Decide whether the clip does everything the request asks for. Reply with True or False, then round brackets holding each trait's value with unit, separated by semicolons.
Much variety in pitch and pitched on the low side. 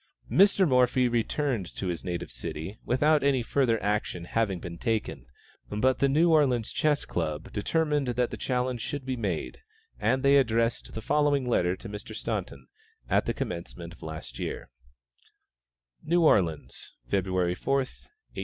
True (7.2 semitones; 120 Hz)